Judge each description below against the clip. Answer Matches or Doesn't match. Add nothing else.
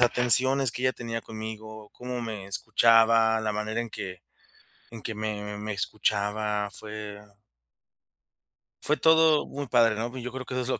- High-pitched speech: Doesn't match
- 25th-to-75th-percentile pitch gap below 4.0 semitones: Matches